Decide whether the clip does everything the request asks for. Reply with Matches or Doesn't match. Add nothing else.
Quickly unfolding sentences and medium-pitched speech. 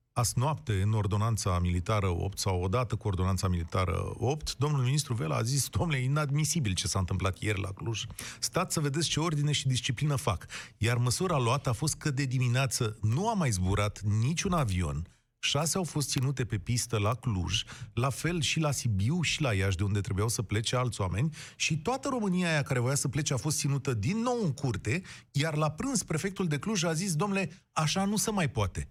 Doesn't match